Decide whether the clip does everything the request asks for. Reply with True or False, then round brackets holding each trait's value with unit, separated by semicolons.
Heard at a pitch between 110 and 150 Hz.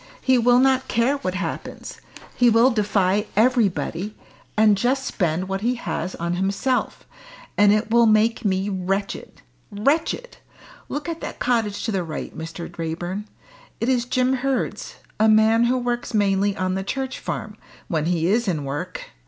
False (210 Hz)